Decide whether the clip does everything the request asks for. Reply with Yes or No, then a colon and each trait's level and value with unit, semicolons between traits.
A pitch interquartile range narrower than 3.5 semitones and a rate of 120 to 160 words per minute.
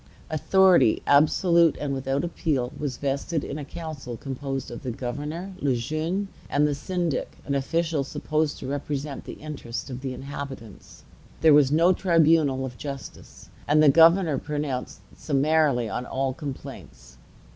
Yes: average, 2.9 semitones; average, 145 wpm